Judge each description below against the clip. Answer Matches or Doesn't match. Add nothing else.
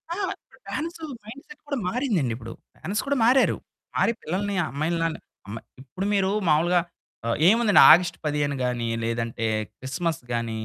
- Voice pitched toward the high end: Doesn't match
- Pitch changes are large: Matches